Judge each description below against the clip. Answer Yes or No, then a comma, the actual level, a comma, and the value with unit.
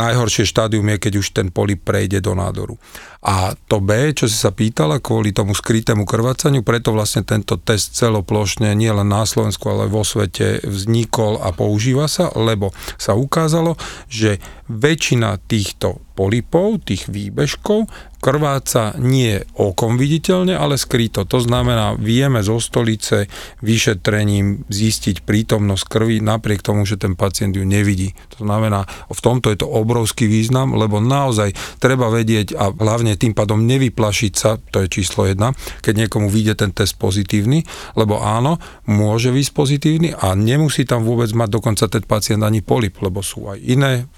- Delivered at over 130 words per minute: Yes, average, 160 wpm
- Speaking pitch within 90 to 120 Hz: Yes, low, 110 Hz